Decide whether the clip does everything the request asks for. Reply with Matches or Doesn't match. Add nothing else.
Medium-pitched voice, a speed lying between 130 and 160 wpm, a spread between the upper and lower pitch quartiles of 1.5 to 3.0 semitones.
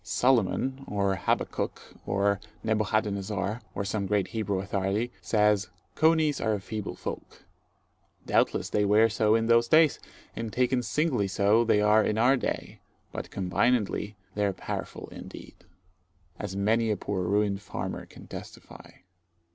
Doesn't match